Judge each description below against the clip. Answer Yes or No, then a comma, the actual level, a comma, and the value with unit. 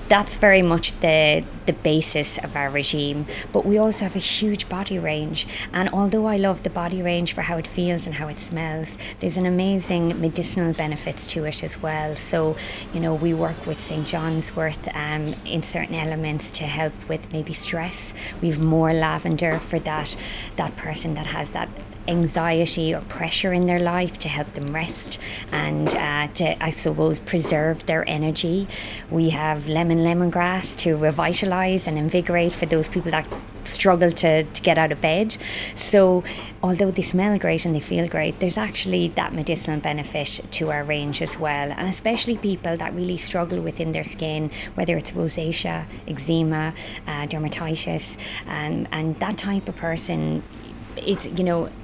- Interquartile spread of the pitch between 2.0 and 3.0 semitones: Yes, narrow, 2.6 semitones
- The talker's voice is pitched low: No, medium, 160 Hz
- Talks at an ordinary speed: Yes, average, 170 wpm